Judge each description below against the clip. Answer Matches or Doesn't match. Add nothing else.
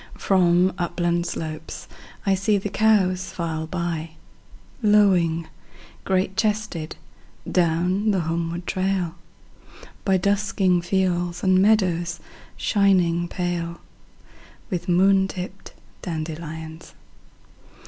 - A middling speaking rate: Doesn't match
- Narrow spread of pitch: Matches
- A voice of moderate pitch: Matches